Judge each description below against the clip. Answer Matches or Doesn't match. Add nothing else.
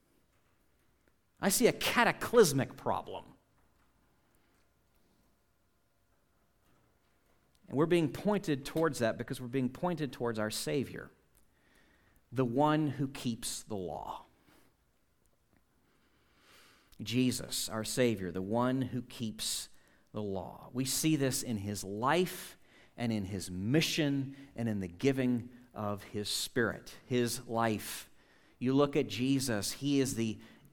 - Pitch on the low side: Matches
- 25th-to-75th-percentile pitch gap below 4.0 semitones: Doesn't match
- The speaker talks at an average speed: Doesn't match